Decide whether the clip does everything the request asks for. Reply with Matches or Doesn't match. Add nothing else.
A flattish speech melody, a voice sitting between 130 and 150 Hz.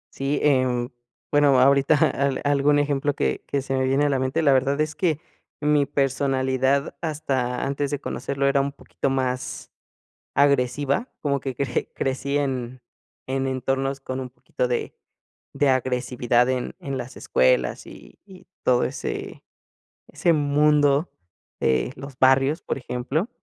Matches